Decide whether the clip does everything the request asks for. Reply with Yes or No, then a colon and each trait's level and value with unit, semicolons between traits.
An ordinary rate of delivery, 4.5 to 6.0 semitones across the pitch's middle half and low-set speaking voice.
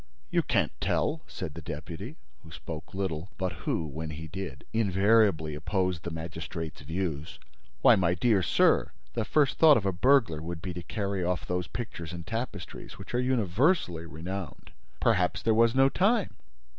Yes: average, 170 wpm; wide, 5.4 semitones; very low, 90 Hz